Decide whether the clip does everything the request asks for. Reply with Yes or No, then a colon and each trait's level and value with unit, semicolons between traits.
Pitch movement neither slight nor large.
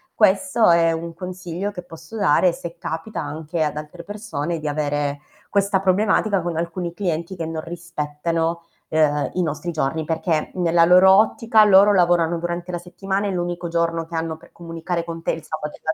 No: narrow, 2.2 semitones